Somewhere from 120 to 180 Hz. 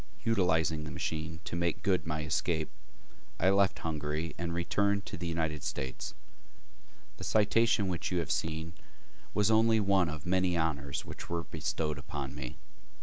No: very low, 85 Hz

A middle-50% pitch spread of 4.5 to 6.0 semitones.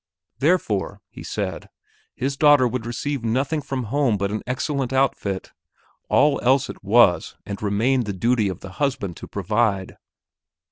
Yes: average, 5.1 semitones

